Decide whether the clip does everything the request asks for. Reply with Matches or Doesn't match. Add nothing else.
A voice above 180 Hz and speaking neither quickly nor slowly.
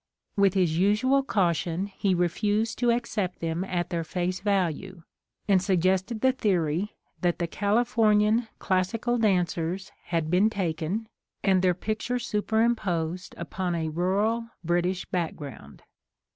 Doesn't match